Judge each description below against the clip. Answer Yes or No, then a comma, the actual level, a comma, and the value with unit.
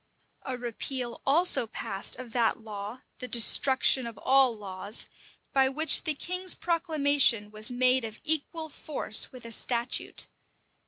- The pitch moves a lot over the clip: No, average, 4.1 semitones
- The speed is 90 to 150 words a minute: Yes, average, 140 wpm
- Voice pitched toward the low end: No, very high, 255 Hz